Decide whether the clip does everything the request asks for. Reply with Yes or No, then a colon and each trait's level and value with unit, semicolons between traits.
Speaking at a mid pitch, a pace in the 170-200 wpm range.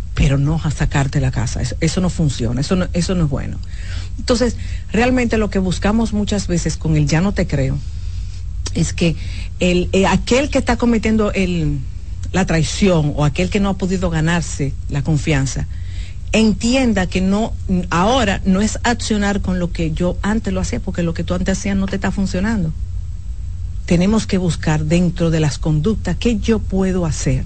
Yes: medium, 160 Hz; average, 185 wpm